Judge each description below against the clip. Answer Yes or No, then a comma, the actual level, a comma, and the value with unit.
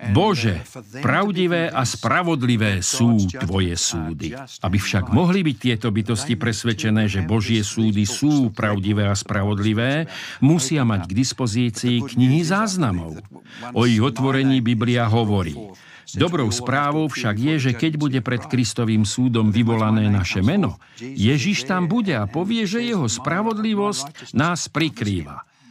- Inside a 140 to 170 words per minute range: No, average, 130 wpm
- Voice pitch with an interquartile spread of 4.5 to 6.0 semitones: Yes, average, 5.1 semitones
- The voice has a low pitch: Yes, low, 120 Hz